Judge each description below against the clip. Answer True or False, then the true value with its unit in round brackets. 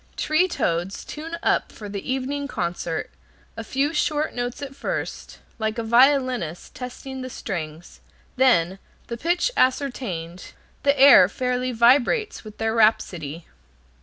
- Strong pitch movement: True (6.2 semitones)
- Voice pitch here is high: True (245 Hz)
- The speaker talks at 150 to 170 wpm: False (135 wpm)